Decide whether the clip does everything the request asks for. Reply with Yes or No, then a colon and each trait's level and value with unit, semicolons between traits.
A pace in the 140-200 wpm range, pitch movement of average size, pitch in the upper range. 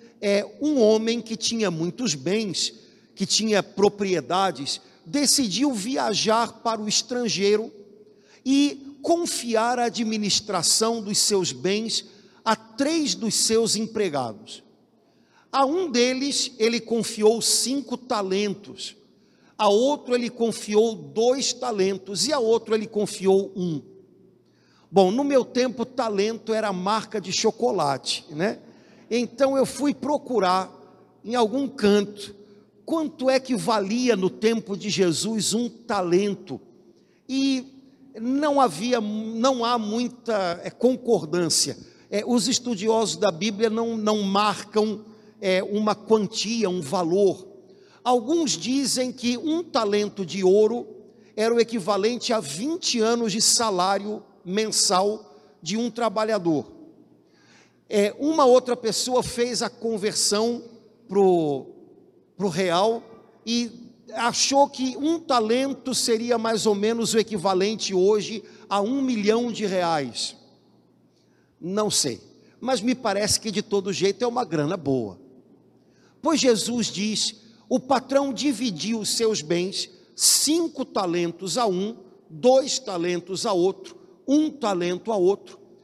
No: slow, 120 wpm; average, 3.4 semitones; high, 220 Hz